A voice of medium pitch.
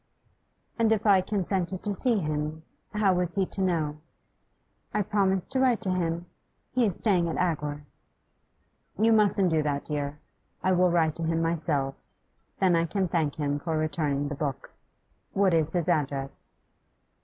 Yes: medium, 170 Hz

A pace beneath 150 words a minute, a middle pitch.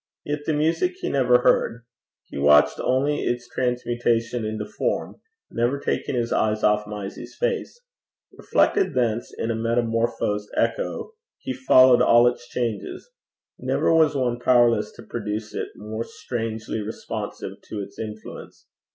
No: average, 140 wpm; low, 120 Hz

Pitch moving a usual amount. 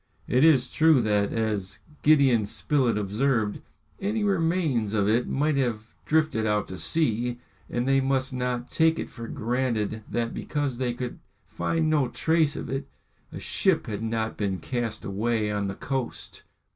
Yes: average, 4.4 semitones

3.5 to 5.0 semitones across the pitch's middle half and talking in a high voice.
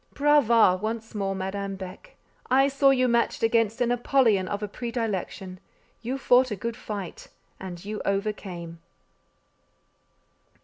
Yes: average, 4.0 semitones; high, 215 Hz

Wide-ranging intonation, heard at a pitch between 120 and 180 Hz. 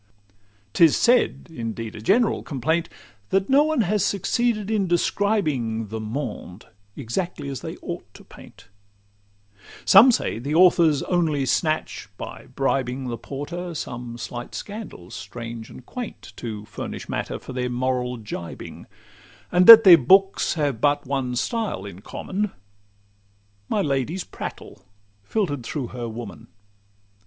Yes: wide, 8.0 semitones; medium, 140 Hz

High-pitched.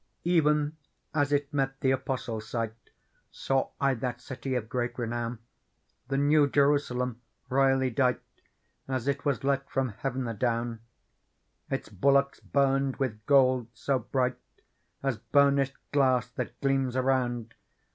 No: low, 130 Hz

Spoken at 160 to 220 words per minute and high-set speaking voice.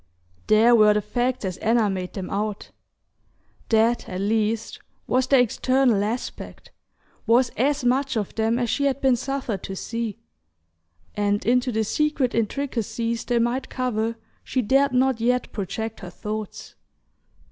No: average, 145 wpm; high, 230 Hz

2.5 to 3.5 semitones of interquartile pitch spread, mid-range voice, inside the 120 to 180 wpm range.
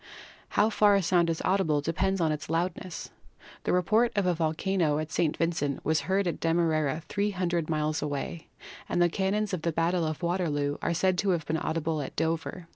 No: average, 3.0 semitones; medium, 170 Hz; average, 195 wpm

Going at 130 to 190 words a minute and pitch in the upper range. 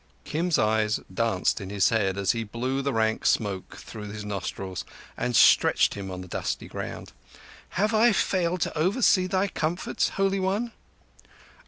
No: average, 160 wpm; low, 115 Hz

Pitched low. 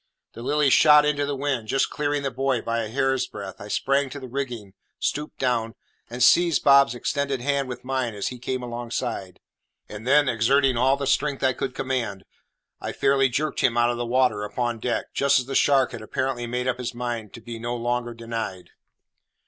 Yes: low, 125 Hz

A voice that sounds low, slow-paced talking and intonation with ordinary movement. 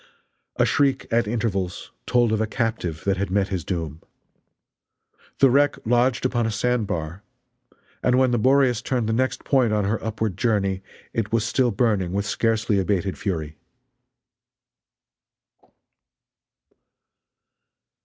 Yes: low, 110 Hz; slow, 130 wpm; average, 3.8 semitones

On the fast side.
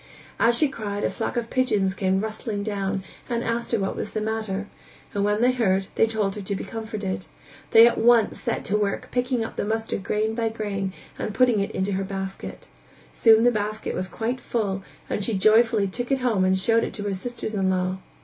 Yes: fast, 215 wpm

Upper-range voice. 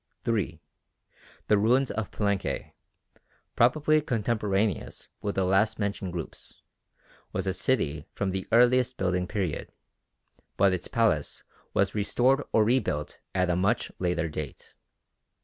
No: low, 100 Hz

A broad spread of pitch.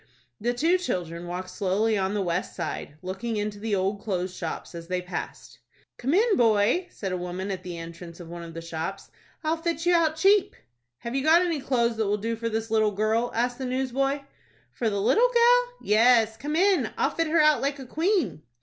Yes: wide, 8.2 semitones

